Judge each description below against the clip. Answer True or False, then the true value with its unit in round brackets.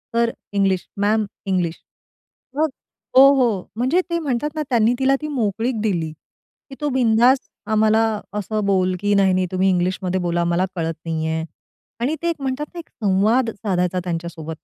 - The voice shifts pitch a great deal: True (5.7 semitones)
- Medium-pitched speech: False (210 Hz)